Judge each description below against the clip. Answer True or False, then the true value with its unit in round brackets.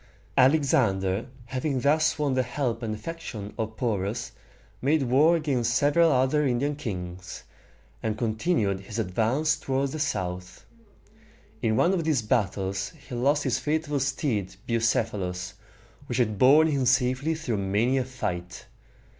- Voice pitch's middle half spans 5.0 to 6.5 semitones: True (5.3 semitones)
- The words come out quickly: False (140 wpm)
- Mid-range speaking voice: False (125 Hz)